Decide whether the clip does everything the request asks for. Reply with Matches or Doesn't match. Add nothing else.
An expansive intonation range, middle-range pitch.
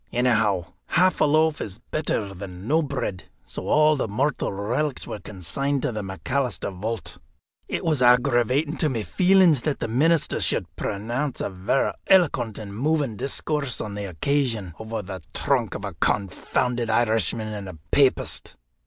Doesn't match